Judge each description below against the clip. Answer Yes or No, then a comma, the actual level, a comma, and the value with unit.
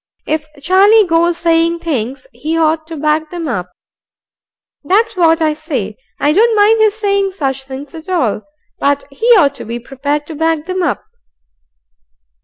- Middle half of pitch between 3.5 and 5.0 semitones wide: Yes, average, 4.4 semitones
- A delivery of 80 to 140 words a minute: No, average, 165 wpm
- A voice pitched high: Yes, very high, 320 Hz